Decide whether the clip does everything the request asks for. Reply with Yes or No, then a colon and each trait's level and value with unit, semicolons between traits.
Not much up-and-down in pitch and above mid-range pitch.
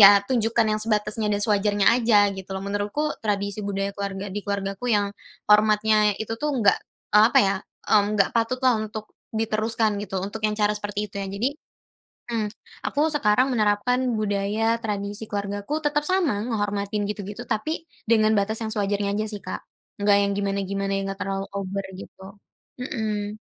Yes: narrow, 1.6 semitones; high, 210 Hz